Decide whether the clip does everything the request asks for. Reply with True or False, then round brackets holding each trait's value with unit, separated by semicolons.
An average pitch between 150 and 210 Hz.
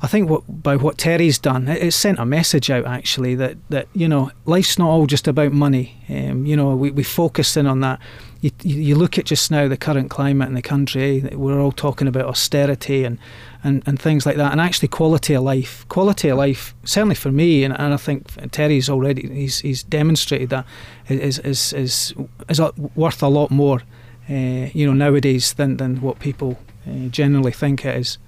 False (140 Hz)